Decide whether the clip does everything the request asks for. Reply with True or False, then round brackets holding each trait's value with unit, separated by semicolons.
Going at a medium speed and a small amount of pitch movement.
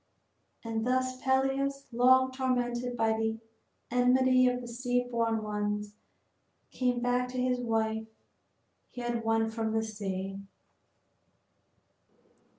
False (115 wpm; 2.3 semitones)